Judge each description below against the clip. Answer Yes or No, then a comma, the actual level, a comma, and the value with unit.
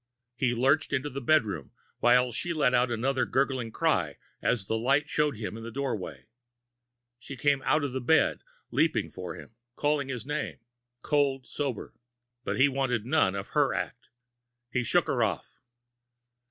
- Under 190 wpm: Yes, average, 165 wpm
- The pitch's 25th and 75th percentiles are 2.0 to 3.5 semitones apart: Yes, average, 3.2 semitones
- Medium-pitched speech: No, low, 130 Hz